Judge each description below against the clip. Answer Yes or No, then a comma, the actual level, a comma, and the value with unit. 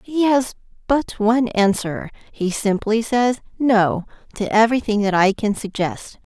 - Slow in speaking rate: Yes, slow, 130 wpm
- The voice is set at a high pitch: Yes, high, 220 Hz